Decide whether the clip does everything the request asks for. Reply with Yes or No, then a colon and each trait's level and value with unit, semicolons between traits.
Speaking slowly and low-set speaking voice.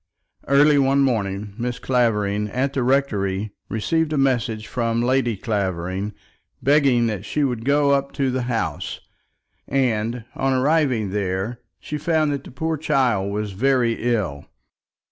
No: average, 145 wpm; low, 120 Hz